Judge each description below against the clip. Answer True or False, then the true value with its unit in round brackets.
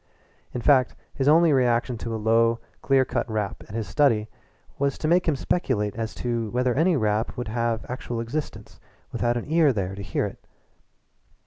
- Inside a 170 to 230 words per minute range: True (185 wpm)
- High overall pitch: False (120 Hz)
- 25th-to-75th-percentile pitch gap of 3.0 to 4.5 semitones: True (3.6 semitones)